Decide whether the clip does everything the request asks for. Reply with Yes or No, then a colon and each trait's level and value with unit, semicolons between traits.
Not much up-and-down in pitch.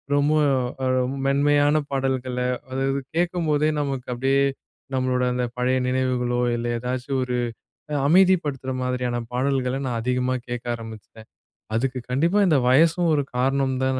Yes: narrow, 2.1 semitones